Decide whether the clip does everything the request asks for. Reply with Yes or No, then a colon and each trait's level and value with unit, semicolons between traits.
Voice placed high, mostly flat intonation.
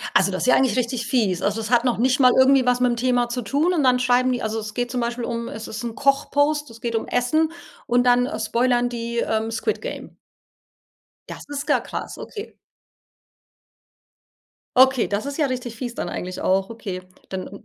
Yes: high, 245 Hz; narrow, 2.3 semitones